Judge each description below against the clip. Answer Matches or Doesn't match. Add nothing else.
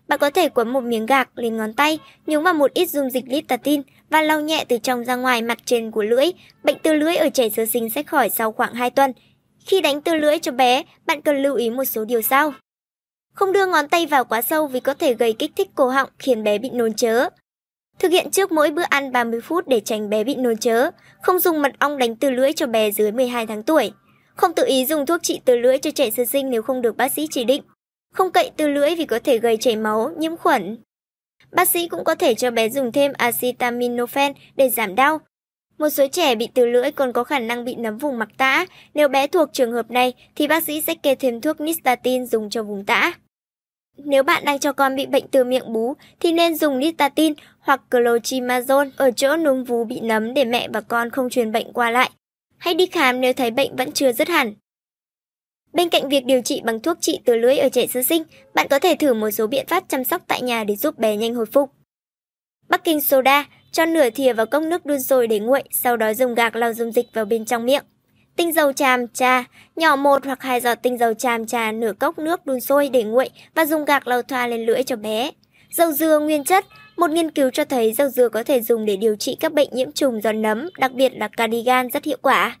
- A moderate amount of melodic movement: Matches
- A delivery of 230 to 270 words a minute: Matches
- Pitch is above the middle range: Matches